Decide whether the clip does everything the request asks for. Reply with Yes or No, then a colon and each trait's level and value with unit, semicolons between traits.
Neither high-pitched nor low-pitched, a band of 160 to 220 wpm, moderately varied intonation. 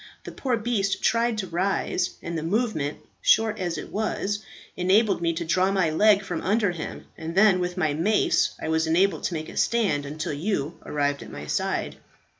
Yes: medium, 180 Hz; average, 195 wpm; average, 4.6 semitones